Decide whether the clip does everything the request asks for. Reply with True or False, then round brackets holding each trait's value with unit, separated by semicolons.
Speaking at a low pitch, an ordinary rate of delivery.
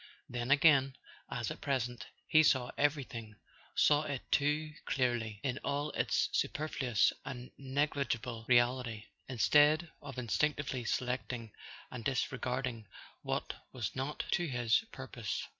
False (130 Hz; 120 wpm)